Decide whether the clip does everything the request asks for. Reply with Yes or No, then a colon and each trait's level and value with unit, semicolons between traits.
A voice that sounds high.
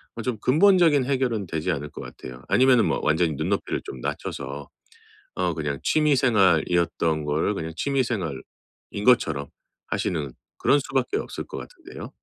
No: very low, 90 Hz